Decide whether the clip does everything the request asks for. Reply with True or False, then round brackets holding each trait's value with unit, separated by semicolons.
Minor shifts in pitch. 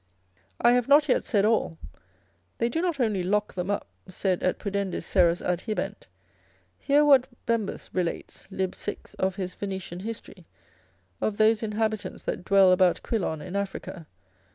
False (3.6 semitones)